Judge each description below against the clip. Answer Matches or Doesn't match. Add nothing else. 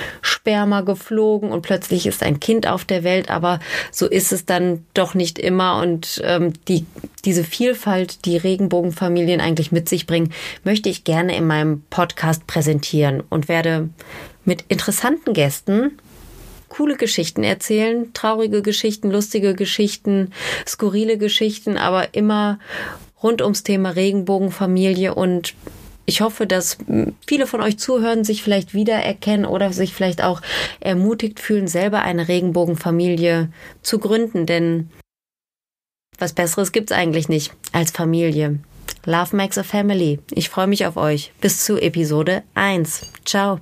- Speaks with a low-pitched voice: Doesn't match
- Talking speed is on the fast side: Doesn't match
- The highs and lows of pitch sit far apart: Doesn't match